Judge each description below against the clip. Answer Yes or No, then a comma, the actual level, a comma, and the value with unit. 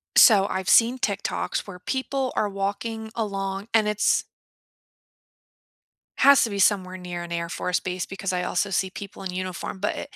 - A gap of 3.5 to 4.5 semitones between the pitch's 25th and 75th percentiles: No, average, 2.8 semitones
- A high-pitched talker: Yes, high, 195 Hz